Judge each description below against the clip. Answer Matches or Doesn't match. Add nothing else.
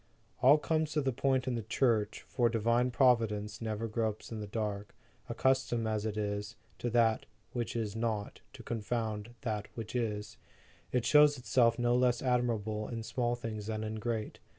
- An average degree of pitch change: Doesn't match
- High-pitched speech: Doesn't match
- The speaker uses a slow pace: Doesn't match